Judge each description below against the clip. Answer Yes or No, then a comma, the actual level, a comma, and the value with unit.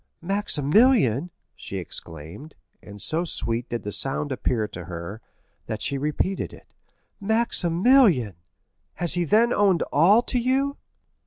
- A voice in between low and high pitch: Yes, medium, 155 Hz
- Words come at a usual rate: No, slow, 115 wpm